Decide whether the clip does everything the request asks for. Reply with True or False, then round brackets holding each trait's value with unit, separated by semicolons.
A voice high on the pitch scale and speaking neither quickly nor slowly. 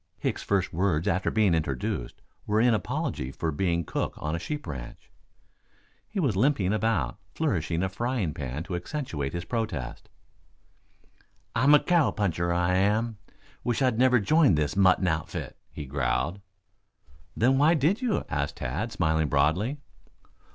False (95 Hz; 145 wpm)